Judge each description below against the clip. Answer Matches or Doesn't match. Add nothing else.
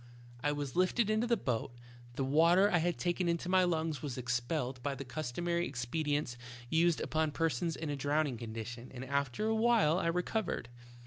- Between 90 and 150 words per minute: Doesn't match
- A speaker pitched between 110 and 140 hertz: Doesn't match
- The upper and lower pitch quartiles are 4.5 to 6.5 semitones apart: Matches